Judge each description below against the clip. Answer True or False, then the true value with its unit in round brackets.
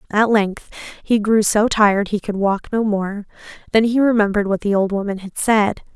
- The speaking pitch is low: False (210 Hz)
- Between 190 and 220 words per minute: True (200 wpm)